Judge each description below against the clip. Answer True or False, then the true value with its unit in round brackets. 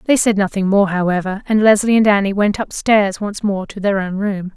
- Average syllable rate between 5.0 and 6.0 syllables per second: True (5.3 syllables/s)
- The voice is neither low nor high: False (200 Hz)